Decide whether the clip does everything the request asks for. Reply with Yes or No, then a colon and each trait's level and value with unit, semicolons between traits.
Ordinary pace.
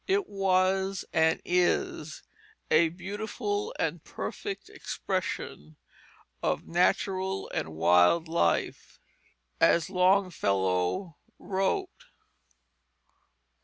No: slow, 75 wpm